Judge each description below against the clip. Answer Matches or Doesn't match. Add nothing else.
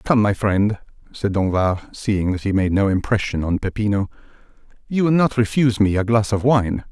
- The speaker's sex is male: Matches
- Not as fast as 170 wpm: Doesn't match